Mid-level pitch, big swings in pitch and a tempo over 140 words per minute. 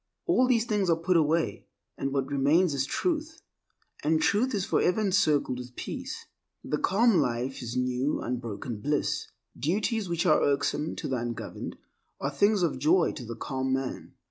Yes: medium, 150 Hz; wide, 6.5 semitones; average, 170 wpm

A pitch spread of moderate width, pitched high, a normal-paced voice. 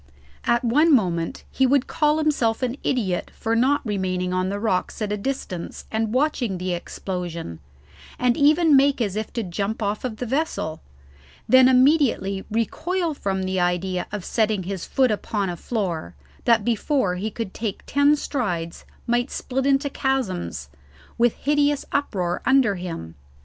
No: wide, 6.3 semitones; high, 220 Hz; average, 155 wpm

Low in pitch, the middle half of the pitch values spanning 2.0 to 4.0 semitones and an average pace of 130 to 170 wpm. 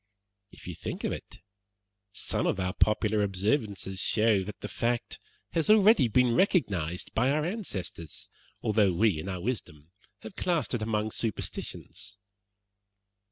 No: low, 110 Hz; average, 4.8 semitones; average, 140 wpm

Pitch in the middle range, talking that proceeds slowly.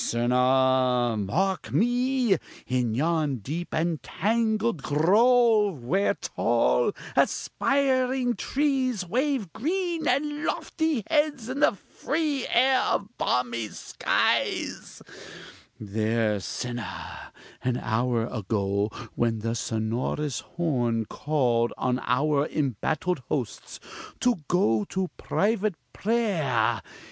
Yes: medium, 160 Hz; slow, 95 wpm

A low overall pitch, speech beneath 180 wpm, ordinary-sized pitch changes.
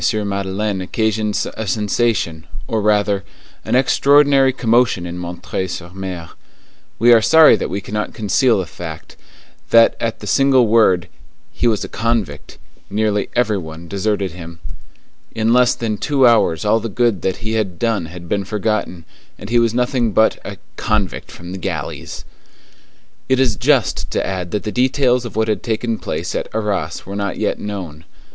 Yes: low, 105 Hz; average, 170 wpm; average, 3.8 semitones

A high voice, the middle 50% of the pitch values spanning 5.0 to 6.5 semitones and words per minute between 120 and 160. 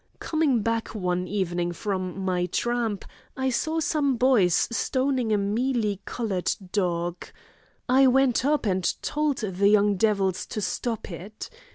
Yes: high, 215 Hz; wide, 5.4 semitones; average, 140 wpm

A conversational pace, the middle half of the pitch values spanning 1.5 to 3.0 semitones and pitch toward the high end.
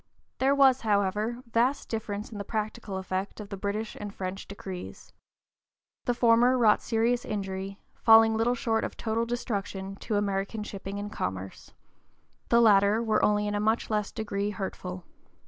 Yes: average, 160 wpm; narrow, 2.5 semitones; high, 210 Hz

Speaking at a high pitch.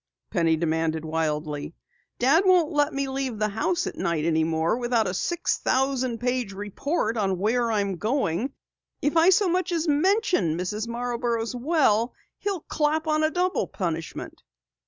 Yes: high, 240 Hz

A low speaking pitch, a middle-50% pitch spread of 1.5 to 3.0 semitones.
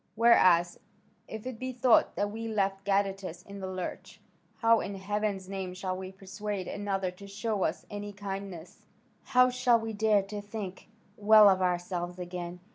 No: high, 200 Hz; narrow, 2.4 semitones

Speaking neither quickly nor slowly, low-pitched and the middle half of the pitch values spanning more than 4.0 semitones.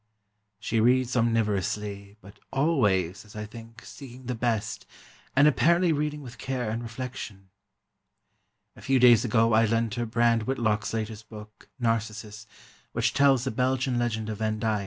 No: average, 155 wpm; low, 115 Hz; average, 2.8 semitones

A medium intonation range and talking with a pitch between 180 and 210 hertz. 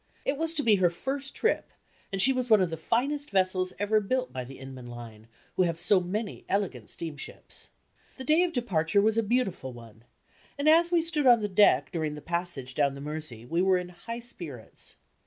No: wide, 8.5 semitones; medium, 185 Hz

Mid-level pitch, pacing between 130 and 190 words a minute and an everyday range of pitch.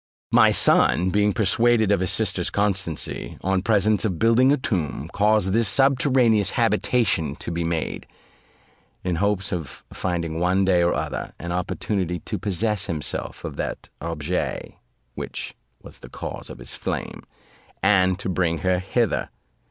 No: very low, 95 Hz; average, 150 wpm; average, 3.6 semitones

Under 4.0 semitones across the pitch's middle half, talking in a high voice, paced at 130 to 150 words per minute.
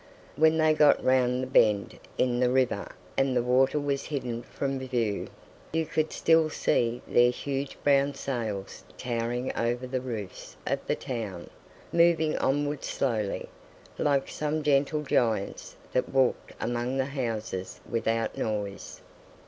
No: average, 3.4 semitones; low, 130 Hz; slow, 135 wpm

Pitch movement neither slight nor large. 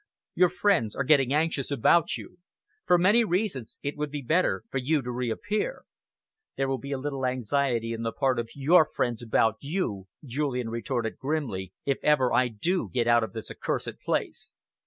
Yes: average, 4.6 semitones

